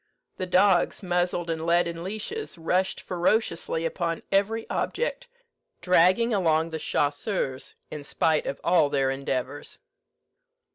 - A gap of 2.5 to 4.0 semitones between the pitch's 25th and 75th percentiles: Yes, average, 3.2 semitones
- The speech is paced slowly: Yes, slow, 125 wpm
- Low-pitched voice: No, medium, 175 Hz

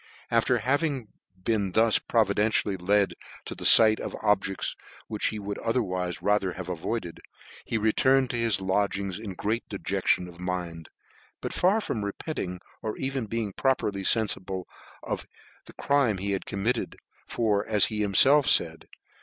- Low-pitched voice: Yes, low, 105 Hz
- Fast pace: No, average, 145 wpm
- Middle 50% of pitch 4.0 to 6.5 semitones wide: No, average, 3.4 semitones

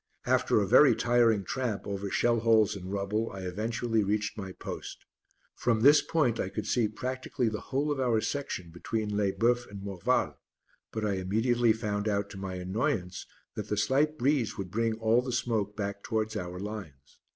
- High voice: No, low, 110 Hz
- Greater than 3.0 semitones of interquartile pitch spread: Yes, average, 3.4 semitones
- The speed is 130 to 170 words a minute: No, average, 180 wpm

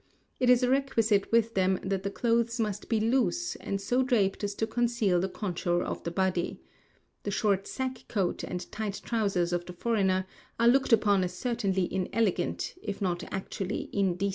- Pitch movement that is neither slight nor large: Yes, average, 3.7 semitones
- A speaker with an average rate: Yes, average, 180 wpm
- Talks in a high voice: Yes, high, 205 Hz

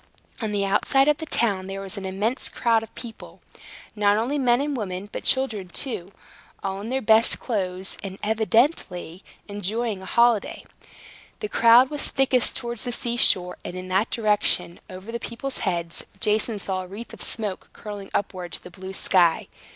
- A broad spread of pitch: No, average, 3.9 semitones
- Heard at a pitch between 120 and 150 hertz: No, high, 210 Hz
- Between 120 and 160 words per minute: No, average, 180 wpm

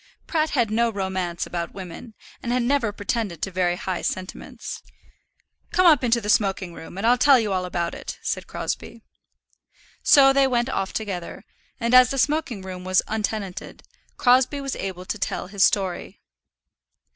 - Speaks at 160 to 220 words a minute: Yes, average, 170 wpm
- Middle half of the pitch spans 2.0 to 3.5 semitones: No, average, 5.1 semitones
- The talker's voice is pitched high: Yes, high, 215 Hz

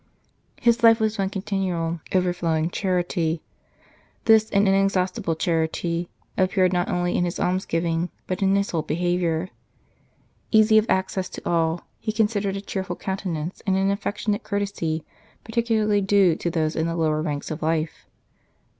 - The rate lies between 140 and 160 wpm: Yes, average, 145 wpm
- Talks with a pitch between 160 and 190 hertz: Yes, medium, 185 Hz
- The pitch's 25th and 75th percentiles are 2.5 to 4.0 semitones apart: Yes, average, 3.3 semitones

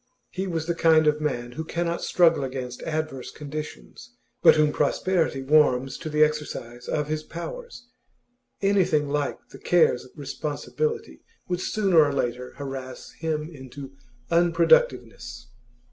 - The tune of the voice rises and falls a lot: No, average, 3.9 semitones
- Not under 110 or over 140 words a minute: Yes, slow, 135 wpm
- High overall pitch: No, medium, 150 Hz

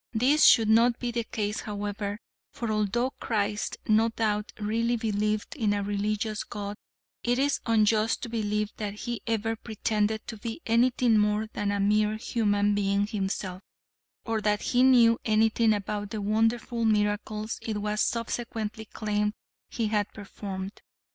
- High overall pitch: Yes, high, 215 Hz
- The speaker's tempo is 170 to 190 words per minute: No, average, 150 wpm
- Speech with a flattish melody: Yes, narrow, 1.7 semitones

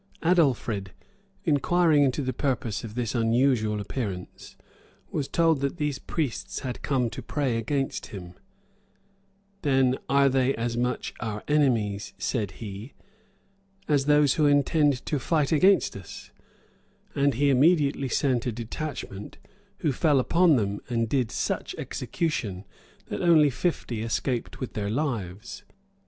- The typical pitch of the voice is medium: No, low, 130 Hz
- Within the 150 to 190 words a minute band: No, slow, 135 wpm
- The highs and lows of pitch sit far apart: No, average, 4.5 semitones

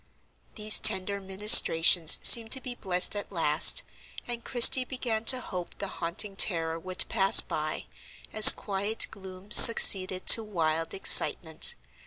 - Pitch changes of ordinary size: Yes, average, 3.6 semitones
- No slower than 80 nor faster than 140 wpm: Yes, slow, 135 wpm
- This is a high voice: Yes, high, 195 Hz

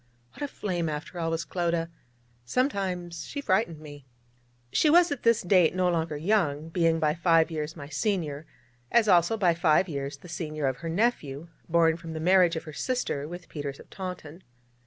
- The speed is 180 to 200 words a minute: Yes, average, 185 wpm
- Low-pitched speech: No, medium, 165 Hz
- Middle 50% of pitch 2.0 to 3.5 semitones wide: Yes, average, 3.2 semitones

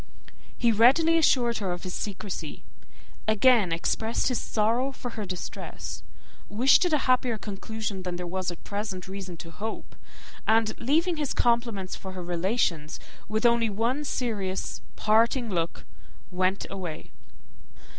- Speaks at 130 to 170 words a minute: Yes, average, 140 wpm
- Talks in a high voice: Yes, high, 215 Hz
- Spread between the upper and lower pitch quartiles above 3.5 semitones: Yes, average, 4.2 semitones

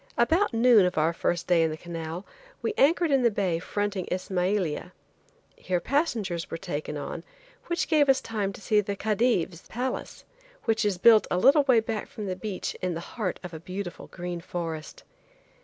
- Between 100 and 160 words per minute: No, average, 185 wpm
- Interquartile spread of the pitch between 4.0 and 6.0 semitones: Yes, average, 4.8 semitones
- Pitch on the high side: Yes, high, 195 Hz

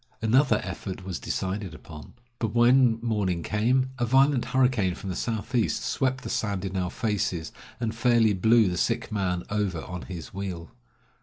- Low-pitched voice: Yes, low, 105 Hz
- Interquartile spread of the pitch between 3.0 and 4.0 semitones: No, average, 4.4 semitones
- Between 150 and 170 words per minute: Yes, average, 165 wpm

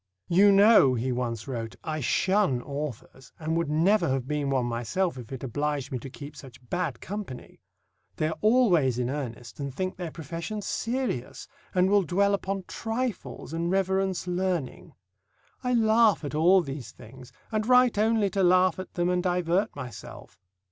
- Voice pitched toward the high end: No, medium, 170 Hz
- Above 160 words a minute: Yes, average, 170 wpm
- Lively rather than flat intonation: Yes, wide, 6.6 semitones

